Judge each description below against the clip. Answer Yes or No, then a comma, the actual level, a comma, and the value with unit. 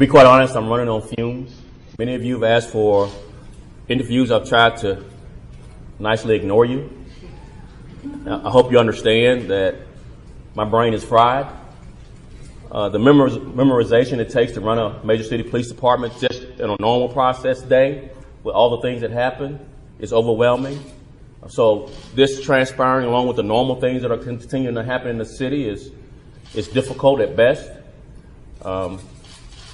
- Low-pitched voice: Yes, low, 120 Hz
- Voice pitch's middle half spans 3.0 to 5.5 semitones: No, narrow, 2.4 semitones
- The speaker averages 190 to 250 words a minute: No, average, 155 wpm